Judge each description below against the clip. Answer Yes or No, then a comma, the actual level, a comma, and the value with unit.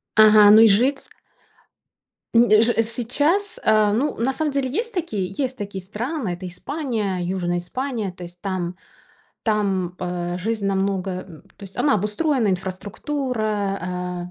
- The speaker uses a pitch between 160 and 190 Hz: No, high, 210 Hz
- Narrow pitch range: No, average, 5.2 semitones